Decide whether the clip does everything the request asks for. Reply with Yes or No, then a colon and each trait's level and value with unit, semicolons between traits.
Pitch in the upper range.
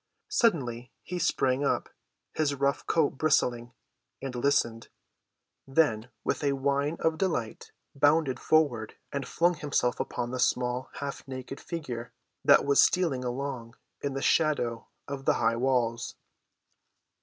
No: low, 135 Hz